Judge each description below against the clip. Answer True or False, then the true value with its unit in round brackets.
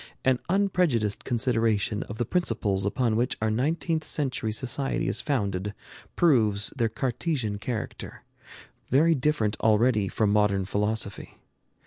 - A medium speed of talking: False (120 wpm)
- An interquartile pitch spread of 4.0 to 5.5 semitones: True (4.4 semitones)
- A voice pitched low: True (115 Hz)